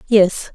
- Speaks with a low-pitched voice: No, high, 200 Hz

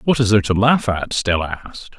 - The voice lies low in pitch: Yes, low, 105 Hz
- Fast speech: Yes, fast, 240 wpm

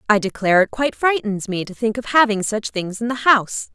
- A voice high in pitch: Yes, high, 220 Hz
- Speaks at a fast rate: Yes, fast, 240 wpm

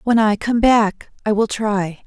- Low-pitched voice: No, high, 215 Hz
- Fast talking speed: No, average, 175 wpm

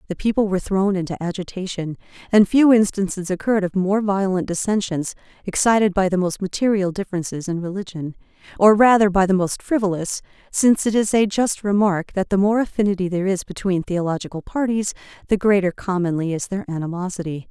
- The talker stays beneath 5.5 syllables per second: No, 5.8 syllables/s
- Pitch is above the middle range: Yes, high, 195 Hz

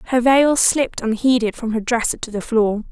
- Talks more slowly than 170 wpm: No, fast, 205 wpm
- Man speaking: No, female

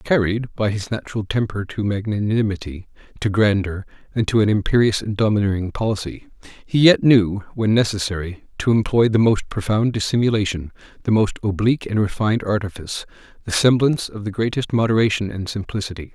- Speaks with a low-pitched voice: Yes, low, 105 Hz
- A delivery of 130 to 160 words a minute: Yes, average, 150 wpm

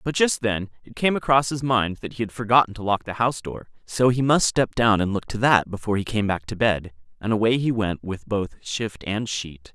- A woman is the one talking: No, male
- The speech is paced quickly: Yes, fast, 250 wpm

